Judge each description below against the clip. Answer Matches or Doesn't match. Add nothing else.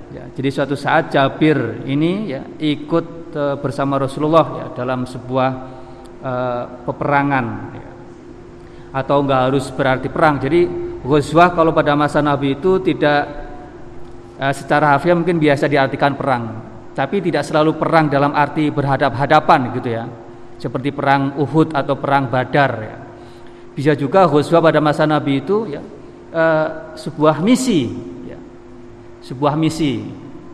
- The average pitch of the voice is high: Doesn't match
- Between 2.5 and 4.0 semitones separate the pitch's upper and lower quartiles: Matches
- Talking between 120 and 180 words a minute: Matches